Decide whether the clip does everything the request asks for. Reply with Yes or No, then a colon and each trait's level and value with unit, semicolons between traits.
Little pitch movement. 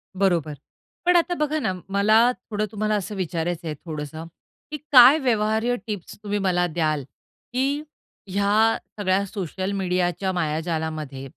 No: average, 4.4 semitones